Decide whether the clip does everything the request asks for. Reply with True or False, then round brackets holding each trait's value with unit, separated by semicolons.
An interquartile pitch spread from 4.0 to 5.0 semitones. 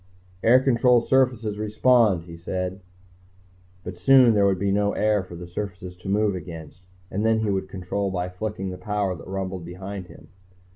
False (2.9 semitones)